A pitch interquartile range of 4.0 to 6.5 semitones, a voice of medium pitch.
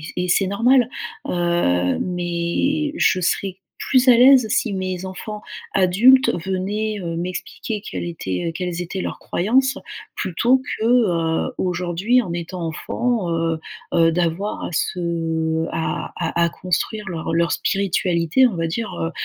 Yes: average, 4.3 semitones; medium, 180 Hz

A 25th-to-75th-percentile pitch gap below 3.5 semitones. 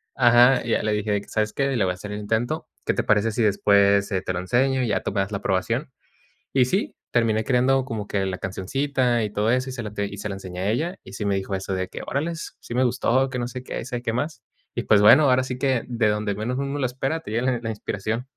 No: average, 4.0 semitones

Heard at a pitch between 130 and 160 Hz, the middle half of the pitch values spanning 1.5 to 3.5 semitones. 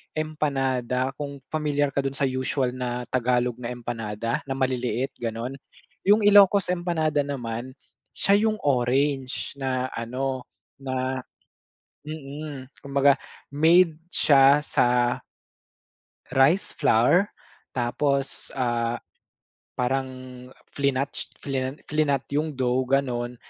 Yes: low, 135 Hz; average, 2.8 semitones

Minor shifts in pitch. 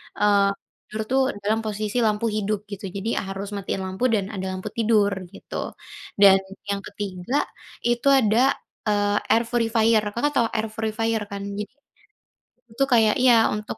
Yes: narrow, 2.0 semitones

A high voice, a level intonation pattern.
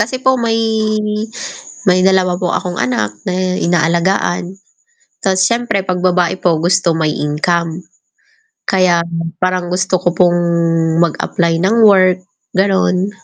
No: medium, 180 Hz; narrow, 1.8 semitones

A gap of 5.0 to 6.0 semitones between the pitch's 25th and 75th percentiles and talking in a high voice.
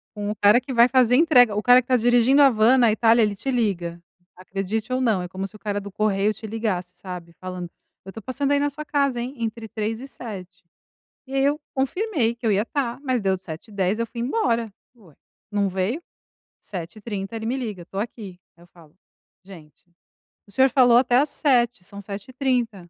No: average, 4.4 semitones; high, 225 Hz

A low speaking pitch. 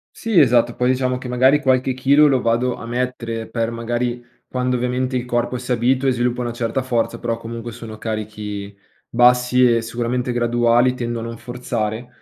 Yes: low, 120 Hz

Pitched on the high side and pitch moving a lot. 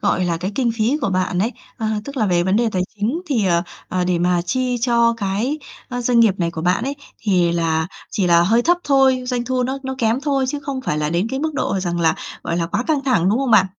Yes: high, 220 Hz; wide, 6.4 semitones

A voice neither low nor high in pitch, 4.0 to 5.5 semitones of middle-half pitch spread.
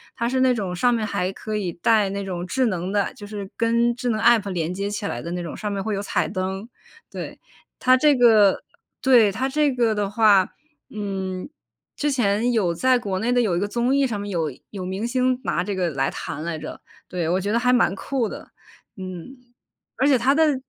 No: high, 210 Hz; average, 4.6 semitones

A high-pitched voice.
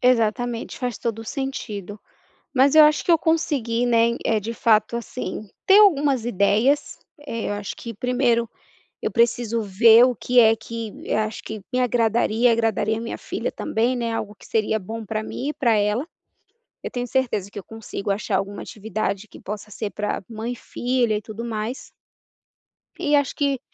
Yes: high, 230 Hz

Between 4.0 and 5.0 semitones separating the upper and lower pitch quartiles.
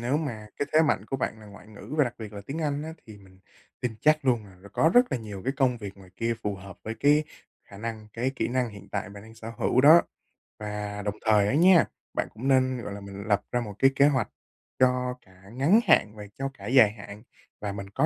Yes: average, 4.7 semitones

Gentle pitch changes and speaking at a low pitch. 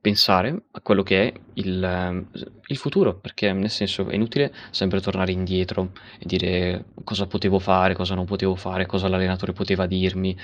Yes: narrow, 1.1 semitones; very low, 95 Hz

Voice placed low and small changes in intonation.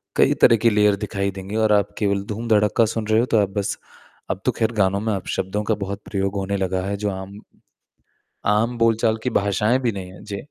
Yes: low, 105 Hz; narrow, 2.0 semitones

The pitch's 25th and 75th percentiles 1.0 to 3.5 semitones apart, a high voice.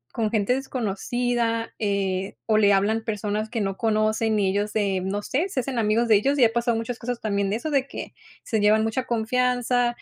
Yes: average, 2.8 semitones; high, 225 Hz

